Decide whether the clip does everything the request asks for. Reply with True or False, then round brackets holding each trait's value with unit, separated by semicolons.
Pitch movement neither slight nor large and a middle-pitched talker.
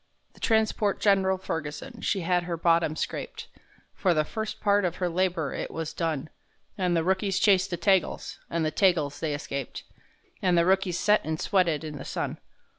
True (3.2 semitones; 180 Hz)